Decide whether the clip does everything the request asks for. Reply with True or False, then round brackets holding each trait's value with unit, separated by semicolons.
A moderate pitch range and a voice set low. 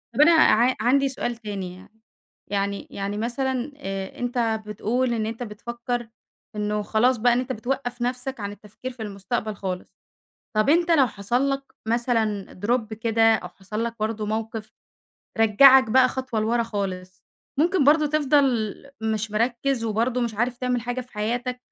False (3.0 semitones; 235 Hz)